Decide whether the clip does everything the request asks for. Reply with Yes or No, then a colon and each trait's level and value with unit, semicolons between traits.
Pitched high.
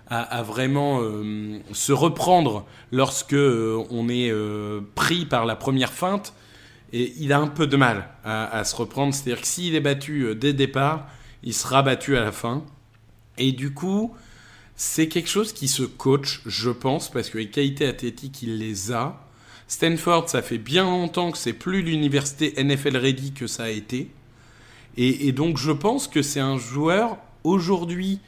No: low, 135 Hz